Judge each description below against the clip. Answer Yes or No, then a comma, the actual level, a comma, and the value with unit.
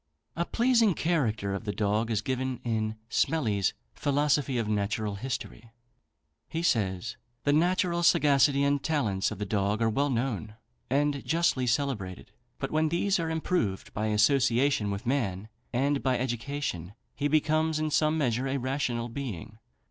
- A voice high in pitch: No, low, 130 Hz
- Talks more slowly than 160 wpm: Yes, average, 150 wpm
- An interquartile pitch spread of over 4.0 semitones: Yes, average, 5.3 semitones